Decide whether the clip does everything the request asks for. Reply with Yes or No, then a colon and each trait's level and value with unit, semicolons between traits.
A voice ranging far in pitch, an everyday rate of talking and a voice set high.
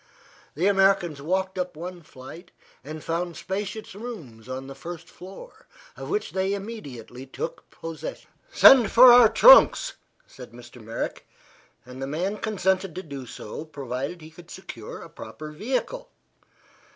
No: wide, 6.1 semitones; average, 145 wpm; medium, 175 Hz